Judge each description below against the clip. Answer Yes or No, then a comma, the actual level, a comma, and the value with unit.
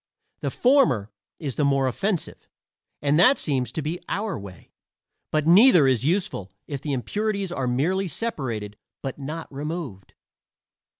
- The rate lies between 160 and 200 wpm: No, average, 140 wpm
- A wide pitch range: Yes, wide, 6.4 semitones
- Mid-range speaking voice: Yes, medium, 150 Hz